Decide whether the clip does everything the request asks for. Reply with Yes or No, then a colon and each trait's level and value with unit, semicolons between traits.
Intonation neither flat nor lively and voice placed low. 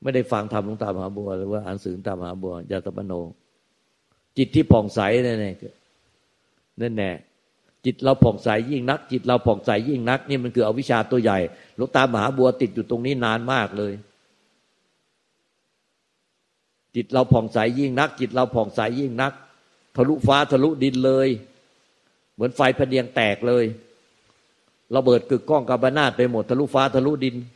Yes: average, 3.9 semitones; low, 125 Hz